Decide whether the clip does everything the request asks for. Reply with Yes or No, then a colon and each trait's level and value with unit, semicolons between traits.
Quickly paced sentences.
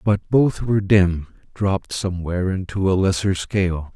No: average, 150 wpm